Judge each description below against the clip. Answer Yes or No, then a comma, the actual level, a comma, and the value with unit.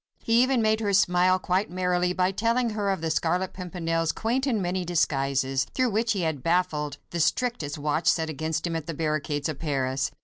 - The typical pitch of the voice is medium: Yes, medium, 175 Hz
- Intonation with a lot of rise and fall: No, average, 4.4 semitones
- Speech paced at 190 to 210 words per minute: Yes, average, 200 wpm